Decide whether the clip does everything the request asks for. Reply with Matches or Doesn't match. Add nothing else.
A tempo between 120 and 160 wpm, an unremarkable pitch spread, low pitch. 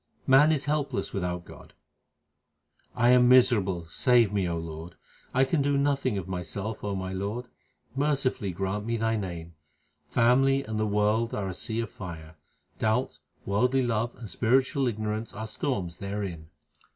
Matches